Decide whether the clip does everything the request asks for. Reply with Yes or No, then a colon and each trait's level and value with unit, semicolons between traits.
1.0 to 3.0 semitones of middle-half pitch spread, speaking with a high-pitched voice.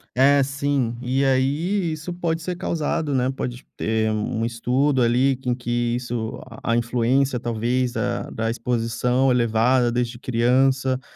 No: narrow, 2.4 semitones; low, 125 Hz